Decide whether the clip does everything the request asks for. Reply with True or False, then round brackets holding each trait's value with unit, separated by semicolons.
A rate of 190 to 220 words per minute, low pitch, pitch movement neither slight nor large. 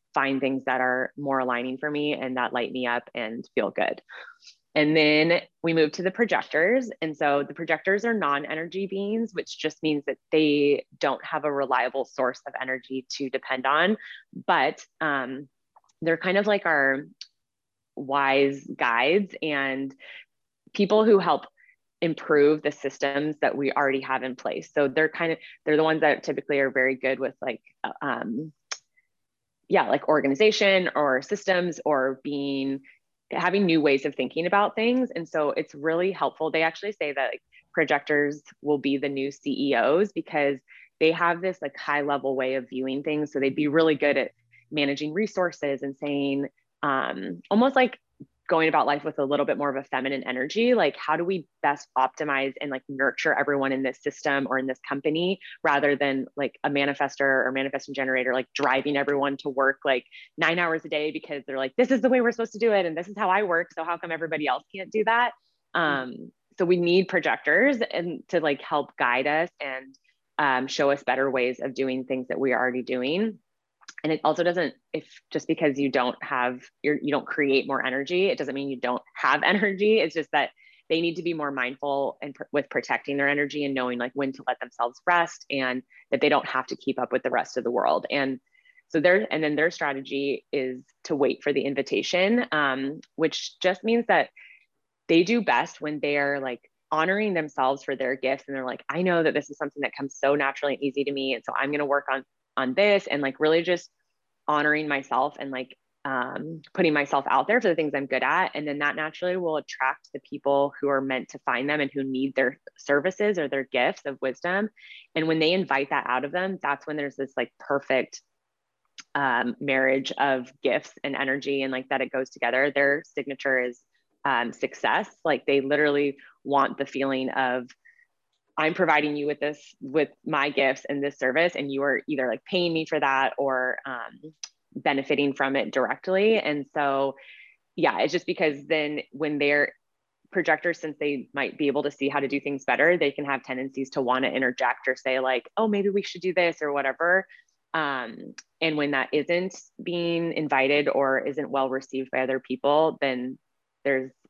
False (200 wpm; 145 Hz; 3.2 semitones)